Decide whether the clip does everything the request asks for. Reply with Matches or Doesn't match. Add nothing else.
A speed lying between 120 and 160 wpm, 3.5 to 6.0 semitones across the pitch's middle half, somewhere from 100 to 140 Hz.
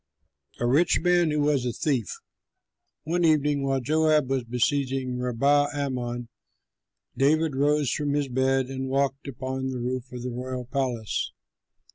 Doesn't match